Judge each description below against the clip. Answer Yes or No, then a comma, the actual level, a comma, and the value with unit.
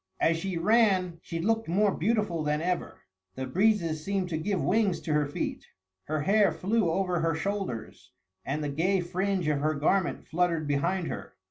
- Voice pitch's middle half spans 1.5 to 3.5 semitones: No, average, 4.0 semitones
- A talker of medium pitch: Yes, medium, 175 Hz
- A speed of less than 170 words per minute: No, average, 175 wpm